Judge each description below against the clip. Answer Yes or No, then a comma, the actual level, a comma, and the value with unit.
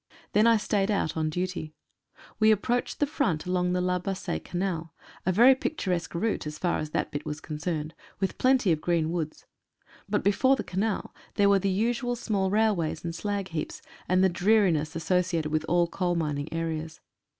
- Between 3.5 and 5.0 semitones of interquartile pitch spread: Yes, average, 4.2 semitones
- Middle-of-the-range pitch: Yes, medium, 180 Hz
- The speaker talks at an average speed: Yes, average, 185 wpm